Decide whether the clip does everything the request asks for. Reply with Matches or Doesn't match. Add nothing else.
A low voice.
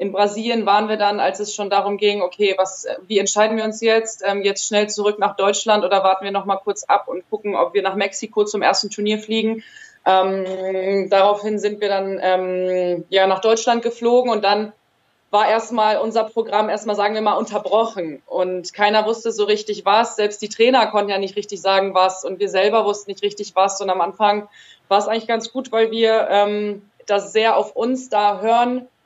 Doesn't match